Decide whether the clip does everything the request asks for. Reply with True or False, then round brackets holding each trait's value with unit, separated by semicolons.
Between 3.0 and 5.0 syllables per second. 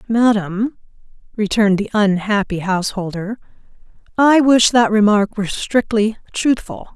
True (4.6 syllables/s)